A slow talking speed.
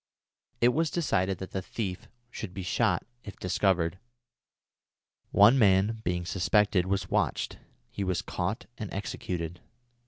Yes: slow, 130 wpm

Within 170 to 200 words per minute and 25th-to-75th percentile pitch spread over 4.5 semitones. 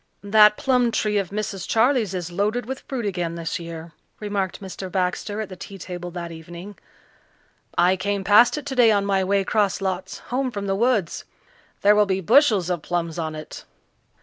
No: average, 185 wpm; average, 3.2 semitones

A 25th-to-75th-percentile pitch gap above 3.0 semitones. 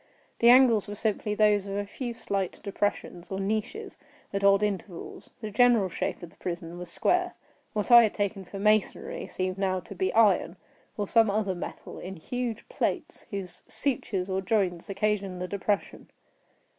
No: narrow, 2.6 semitones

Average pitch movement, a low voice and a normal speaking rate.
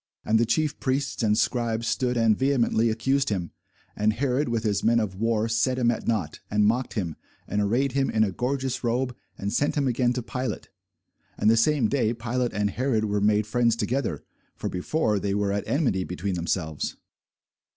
Yes: average, 3.5 semitones; low, 115 Hz; average, 195 wpm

